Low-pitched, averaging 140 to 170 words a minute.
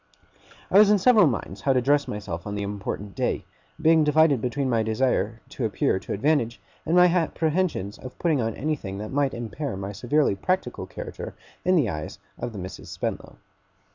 No: low, 130 Hz; average, 185 wpm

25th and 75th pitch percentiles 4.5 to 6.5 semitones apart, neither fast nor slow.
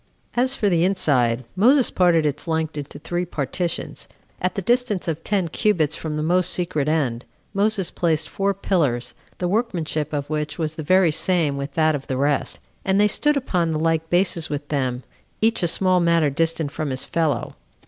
No: average, 3.8 semitones; average, 190 wpm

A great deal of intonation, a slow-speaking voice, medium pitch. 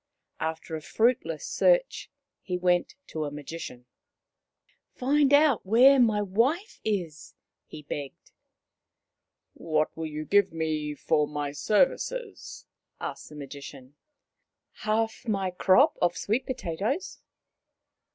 Yes: wide, 7.9 semitones; slow, 125 wpm; medium, 180 Hz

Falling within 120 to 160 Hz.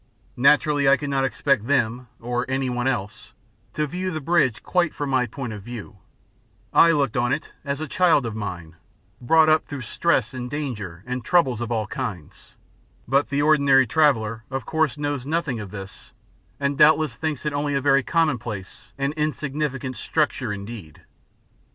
Yes: low, 135 Hz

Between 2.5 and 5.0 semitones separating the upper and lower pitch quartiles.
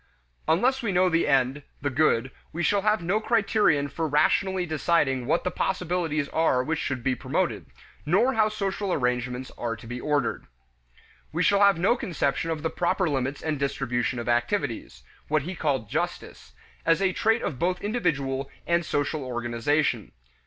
No: wide, 5.6 semitones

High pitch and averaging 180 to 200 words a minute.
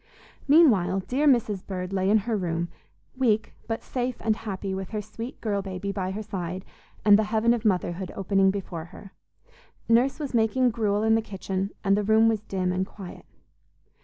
Yes: high, 205 Hz; average, 185 wpm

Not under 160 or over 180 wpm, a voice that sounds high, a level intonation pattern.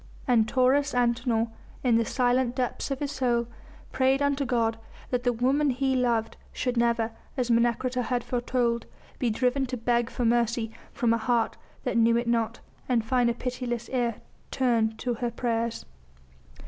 Yes: average, 165 wpm; high, 240 Hz; narrow, 1.5 semitones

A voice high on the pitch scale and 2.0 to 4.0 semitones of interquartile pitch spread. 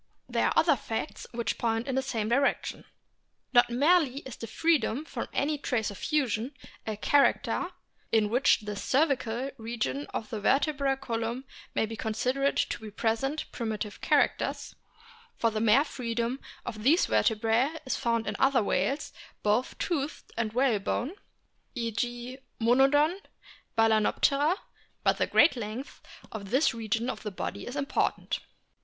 Yes: high, 240 Hz; average, 3.7 semitones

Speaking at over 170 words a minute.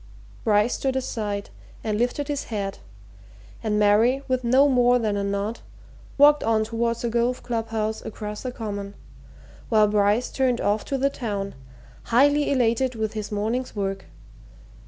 No: average, 155 wpm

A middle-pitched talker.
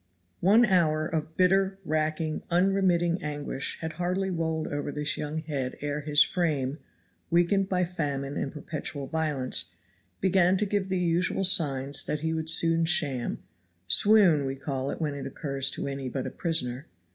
Yes: medium, 160 Hz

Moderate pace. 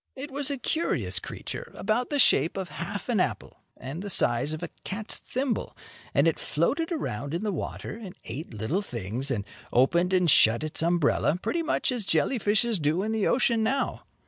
Yes: average, 195 wpm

